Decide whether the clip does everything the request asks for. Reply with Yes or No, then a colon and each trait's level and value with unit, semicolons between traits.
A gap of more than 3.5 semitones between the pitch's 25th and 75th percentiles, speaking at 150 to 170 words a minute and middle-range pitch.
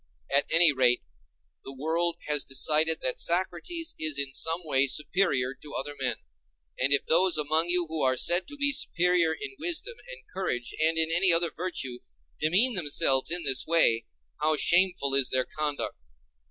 Yes: average, 4.4 semitones; average, 165 wpm; medium, 160 Hz